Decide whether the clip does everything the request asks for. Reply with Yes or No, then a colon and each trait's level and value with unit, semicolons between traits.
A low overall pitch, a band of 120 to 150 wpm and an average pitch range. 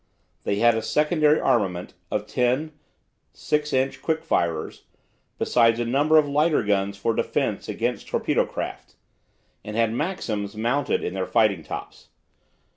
No: low, 115 Hz; average, 140 wpm; wide, 6.3 semitones